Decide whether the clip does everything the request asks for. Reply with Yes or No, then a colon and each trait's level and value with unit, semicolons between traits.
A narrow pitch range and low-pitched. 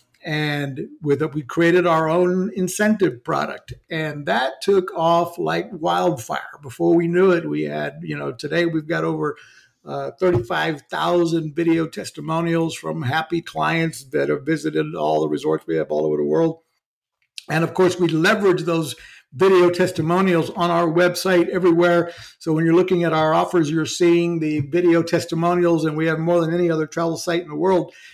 No: narrow, 2.2 semitones; medium, 165 Hz